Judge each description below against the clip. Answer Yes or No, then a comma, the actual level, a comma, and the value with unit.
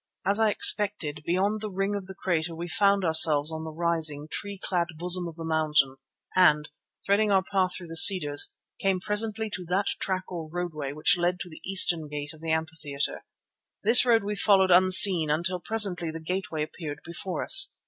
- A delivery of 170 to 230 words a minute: Yes, average, 190 wpm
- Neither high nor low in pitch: Yes, medium, 175 Hz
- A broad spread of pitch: No, average, 3.6 semitones